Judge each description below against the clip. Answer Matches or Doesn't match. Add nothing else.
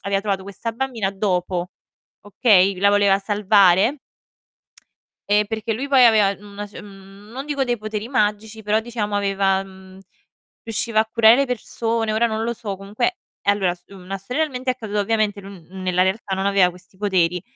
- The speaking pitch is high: Matches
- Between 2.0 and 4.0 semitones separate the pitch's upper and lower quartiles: Matches